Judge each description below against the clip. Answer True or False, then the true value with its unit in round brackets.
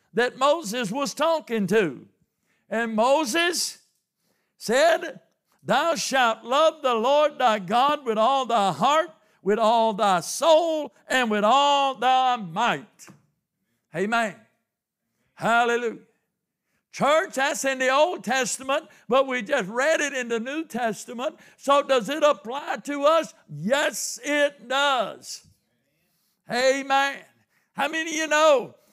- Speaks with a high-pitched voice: True (260 Hz)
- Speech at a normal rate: False (125 wpm)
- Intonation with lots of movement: False (4.4 semitones)